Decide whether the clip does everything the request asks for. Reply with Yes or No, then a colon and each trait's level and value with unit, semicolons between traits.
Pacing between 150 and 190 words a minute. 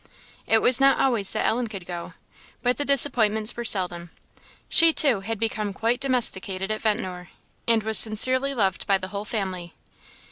Yes: average, 170 wpm